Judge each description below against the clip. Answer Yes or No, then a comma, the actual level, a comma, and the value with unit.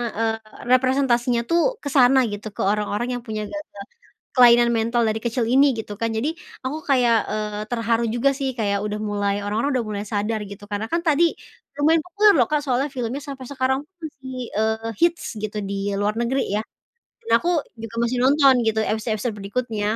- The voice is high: Yes, high, 235 Hz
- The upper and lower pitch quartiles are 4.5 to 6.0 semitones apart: No, average, 3.8 semitones